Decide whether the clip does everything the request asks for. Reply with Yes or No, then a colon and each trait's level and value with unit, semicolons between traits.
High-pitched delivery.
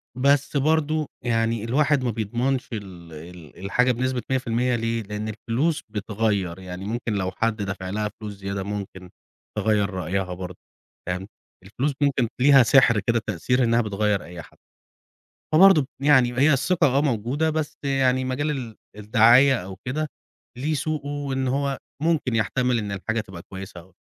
No: low, 115 Hz